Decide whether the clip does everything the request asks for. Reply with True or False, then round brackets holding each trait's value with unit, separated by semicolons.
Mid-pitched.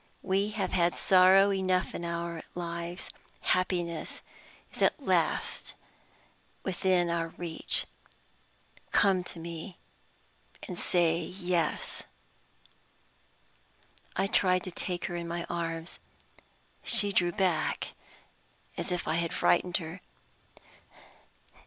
True (175 Hz)